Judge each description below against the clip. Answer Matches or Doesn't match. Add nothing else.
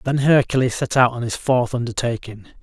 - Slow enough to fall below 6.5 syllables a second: Matches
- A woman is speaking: Doesn't match